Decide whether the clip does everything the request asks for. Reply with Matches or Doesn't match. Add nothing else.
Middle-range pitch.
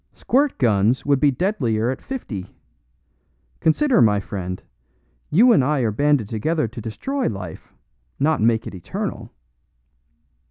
Doesn't match